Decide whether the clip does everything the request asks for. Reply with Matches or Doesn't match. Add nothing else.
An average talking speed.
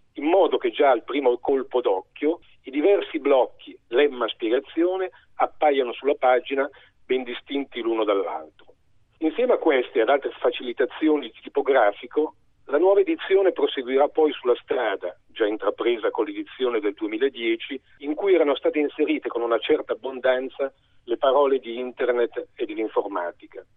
Matches